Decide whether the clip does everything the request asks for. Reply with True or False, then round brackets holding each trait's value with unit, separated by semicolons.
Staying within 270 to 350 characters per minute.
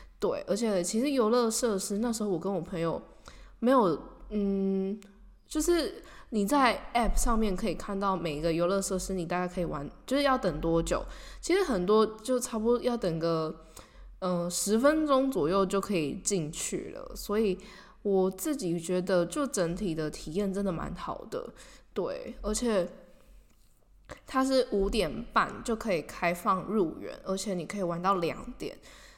False (245 characters per minute)